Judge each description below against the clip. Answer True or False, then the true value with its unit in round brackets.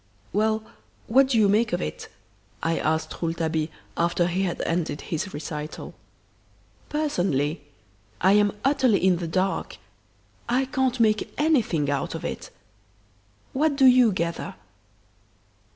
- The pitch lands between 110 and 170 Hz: False (195 Hz)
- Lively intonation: True (7.0 semitones)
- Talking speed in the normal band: False (130 wpm)